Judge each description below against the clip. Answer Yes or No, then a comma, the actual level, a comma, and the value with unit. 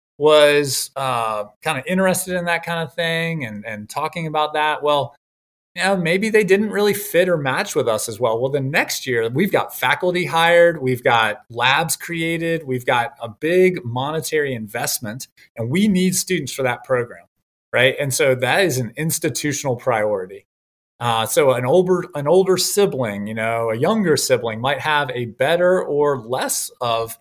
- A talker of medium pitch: Yes, medium, 150 Hz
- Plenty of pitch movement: Yes, wide, 5.7 semitones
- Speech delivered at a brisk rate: No, average, 180 wpm